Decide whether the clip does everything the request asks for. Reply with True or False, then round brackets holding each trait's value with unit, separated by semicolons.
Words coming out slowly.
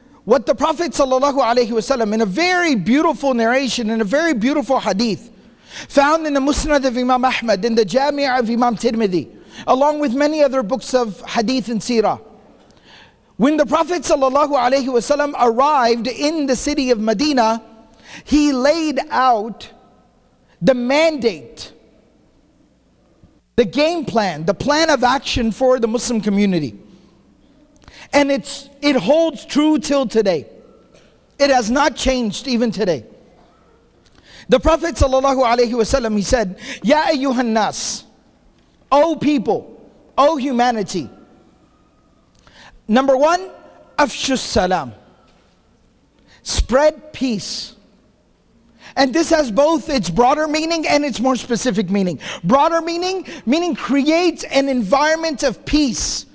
True (120 wpm)